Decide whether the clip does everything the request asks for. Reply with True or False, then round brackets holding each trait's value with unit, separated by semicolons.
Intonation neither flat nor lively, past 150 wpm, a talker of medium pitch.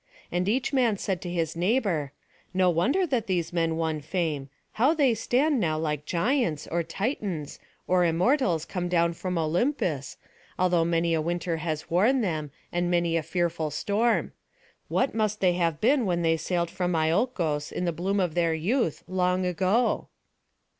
True (4.1 semitones; 165 wpm; 175 Hz)